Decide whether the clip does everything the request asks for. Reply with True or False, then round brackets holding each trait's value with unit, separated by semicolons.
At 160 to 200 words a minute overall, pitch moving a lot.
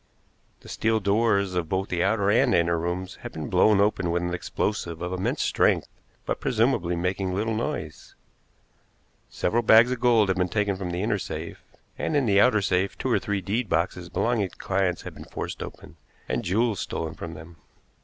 False (195 wpm; 3.8 semitones)